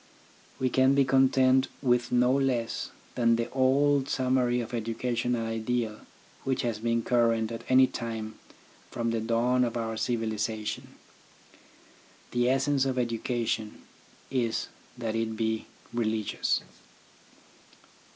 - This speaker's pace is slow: Yes, slow, 120 wpm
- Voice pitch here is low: Yes, low, 120 Hz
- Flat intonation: Yes, narrow, 2.3 semitones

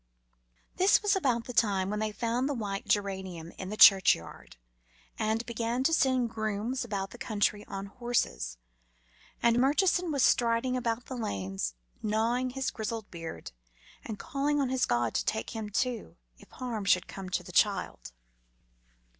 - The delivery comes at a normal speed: Yes, average, 160 wpm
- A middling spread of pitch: Yes, average, 4.2 semitones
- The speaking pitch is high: Yes, high, 225 Hz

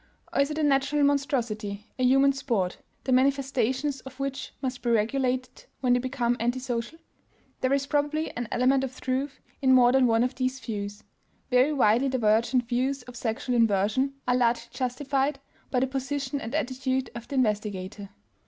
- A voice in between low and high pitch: No, very high, 255 Hz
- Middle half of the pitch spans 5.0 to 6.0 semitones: No, narrow, 2.5 semitones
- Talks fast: No, average, 170 wpm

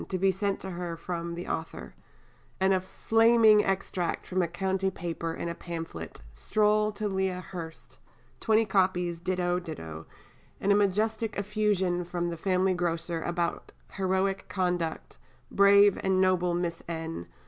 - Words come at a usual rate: Yes, average, 150 wpm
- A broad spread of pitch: No, narrow, 2.4 semitones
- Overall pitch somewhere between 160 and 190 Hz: Yes, medium, 185 Hz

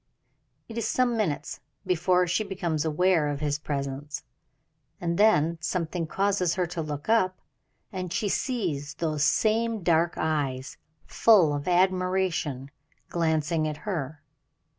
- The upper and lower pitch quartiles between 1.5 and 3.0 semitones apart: No, average, 3.8 semitones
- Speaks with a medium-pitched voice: Yes, medium, 170 Hz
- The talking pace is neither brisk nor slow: No, slow, 130 wpm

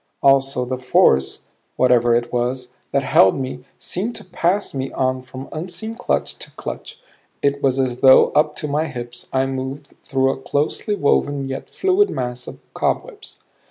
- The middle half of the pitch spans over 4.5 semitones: No, average, 2.9 semitones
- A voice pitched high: No, low, 135 Hz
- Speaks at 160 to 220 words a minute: Yes, average, 165 wpm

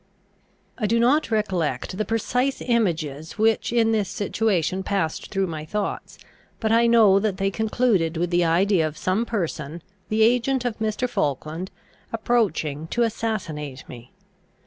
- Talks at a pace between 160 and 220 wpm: No, average, 145 wpm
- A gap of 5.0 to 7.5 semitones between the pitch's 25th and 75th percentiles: Yes, wide, 5.6 semitones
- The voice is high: Yes, high, 200 Hz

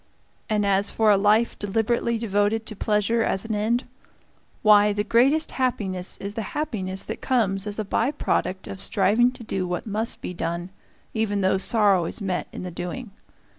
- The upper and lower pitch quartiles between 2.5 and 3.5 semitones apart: Yes, average, 2.8 semitones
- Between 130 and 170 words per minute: No, average, 180 wpm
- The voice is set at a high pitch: Yes, high, 210 Hz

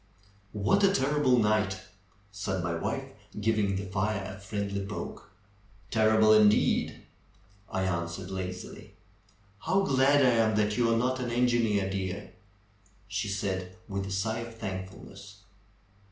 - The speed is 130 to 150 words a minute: Yes, average, 140 wpm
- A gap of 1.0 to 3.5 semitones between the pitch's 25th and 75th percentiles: Yes, average, 2.9 semitones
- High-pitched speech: No, low, 105 Hz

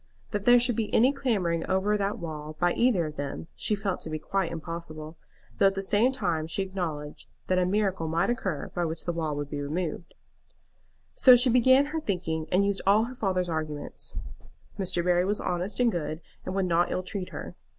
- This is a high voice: No, medium, 180 Hz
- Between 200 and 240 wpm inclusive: Yes, fast, 205 wpm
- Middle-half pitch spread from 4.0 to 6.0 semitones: Yes, average, 4.3 semitones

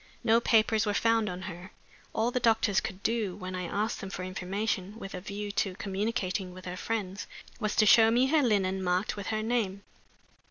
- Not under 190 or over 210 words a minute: Yes, average, 200 wpm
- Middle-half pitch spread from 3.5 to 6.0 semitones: No, average, 3.1 semitones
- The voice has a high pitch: Yes, high, 205 Hz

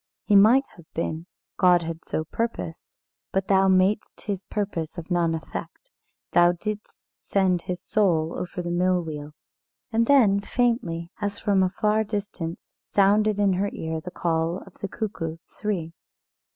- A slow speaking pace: No, average, 155 wpm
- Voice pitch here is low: No, medium, 185 Hz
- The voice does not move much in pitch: No, average, 3.5 semitones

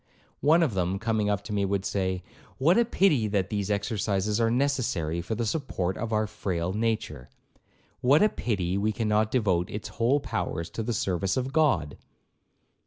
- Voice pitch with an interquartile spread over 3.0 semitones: Yes, average, 4.1 semitones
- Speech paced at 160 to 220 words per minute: Yes, average, 175 wpm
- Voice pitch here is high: No, low, 105 Hz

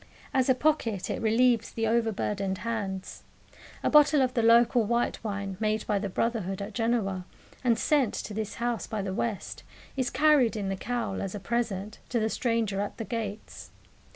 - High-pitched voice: Yes, high, 225 Hz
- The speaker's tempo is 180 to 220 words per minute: Yes, average, 185 wpm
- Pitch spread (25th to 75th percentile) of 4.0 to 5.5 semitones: No, average, 3.1 semitones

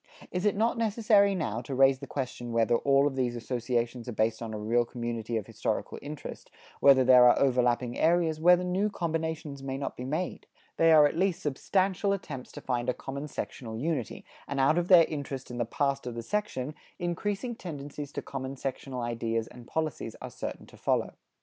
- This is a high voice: No, low, 135 Hz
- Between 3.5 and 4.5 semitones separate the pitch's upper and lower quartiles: No, wide, 5.4 semitones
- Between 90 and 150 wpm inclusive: No, average, 195 wpm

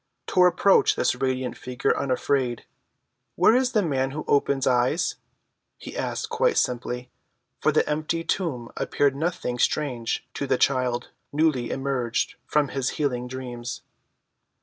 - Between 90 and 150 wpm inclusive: Yes, slow, 135 wpm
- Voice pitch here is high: No, low, 135 Hz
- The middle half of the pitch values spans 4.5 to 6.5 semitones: No, average, 3.8 semitones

